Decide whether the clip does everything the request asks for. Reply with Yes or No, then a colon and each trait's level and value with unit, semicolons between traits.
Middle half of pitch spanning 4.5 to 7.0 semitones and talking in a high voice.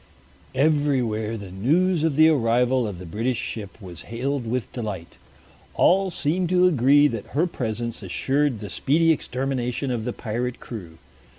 No: average, 4.9 semitones; low, 125 Hz